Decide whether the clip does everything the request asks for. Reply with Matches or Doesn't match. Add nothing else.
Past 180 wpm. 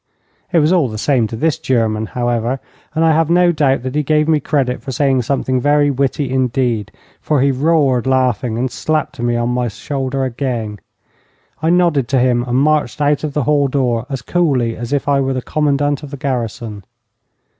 Matches